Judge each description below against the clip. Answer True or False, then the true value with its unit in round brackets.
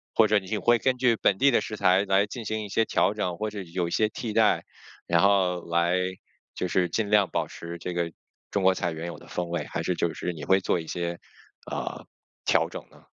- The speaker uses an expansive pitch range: False (3.7 semitones)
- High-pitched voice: False (95 Hz)